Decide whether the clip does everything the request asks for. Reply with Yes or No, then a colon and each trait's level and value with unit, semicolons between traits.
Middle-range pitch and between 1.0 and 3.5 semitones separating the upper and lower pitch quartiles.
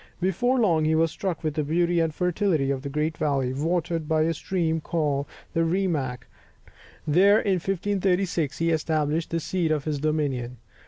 Yes: medium, 160 Hz; average, 3.0 semitones